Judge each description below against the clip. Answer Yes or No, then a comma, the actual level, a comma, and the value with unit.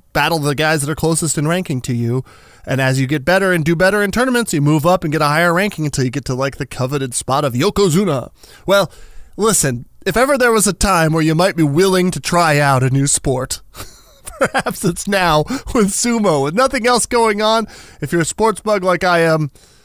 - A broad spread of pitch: Yes, wide, 5.8 semitones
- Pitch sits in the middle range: Yes, medium, 170 Hz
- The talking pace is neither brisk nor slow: No, fast, 225 wpm